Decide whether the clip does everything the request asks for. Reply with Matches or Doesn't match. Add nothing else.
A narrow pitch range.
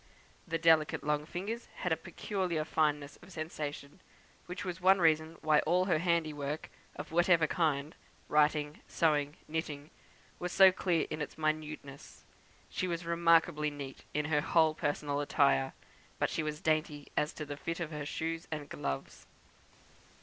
Matches